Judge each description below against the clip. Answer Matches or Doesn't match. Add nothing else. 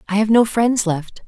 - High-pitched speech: Matches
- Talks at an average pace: Doesn't match